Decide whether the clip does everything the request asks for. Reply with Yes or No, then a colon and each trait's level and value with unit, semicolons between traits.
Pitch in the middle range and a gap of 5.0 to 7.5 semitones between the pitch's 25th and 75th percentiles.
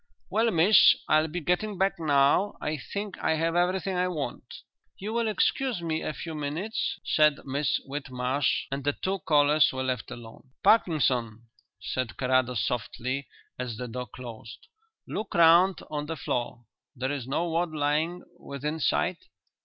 Yes: medium, 150 Hz; average, 5.3 semitones